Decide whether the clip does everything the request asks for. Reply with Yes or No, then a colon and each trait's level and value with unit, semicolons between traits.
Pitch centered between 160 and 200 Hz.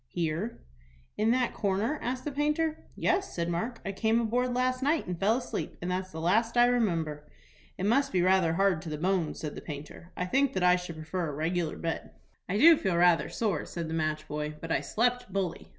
Yes: high, 190 Hz